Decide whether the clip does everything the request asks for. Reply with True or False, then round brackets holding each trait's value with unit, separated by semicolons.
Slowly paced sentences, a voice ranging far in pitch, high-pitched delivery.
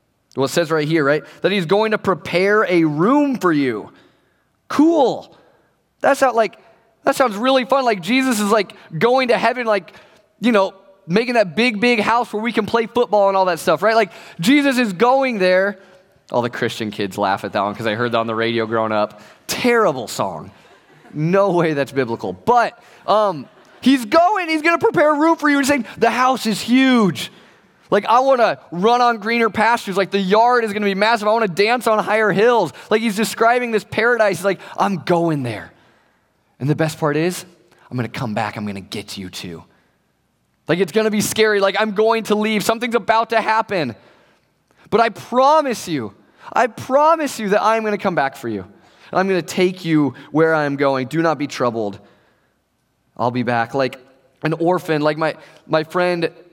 False (205 wpm; 7.1 semitones; 200 Hz)